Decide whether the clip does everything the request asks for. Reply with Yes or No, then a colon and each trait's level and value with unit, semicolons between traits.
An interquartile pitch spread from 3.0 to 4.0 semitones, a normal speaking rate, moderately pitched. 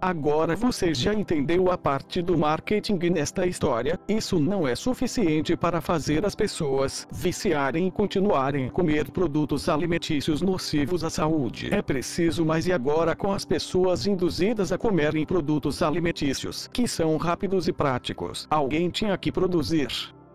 Yes: average, 3.3 semitones; average, 145 wpm; medium, 170 Hz